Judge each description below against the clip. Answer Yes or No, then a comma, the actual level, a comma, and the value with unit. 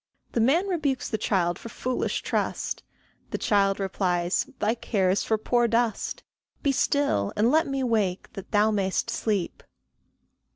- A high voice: Yes, high, 220 Hz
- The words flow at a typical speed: Yes, average, 155 wpm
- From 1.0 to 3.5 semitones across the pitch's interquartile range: No, average, 4.2 semitones